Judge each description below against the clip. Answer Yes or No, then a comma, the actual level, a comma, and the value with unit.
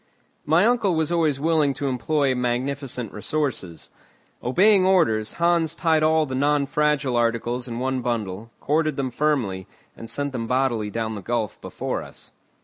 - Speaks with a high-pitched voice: No, low, 135 Hz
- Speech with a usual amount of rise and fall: Yes, average, 4.6 semitones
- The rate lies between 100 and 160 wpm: Yes, average, 155 wpm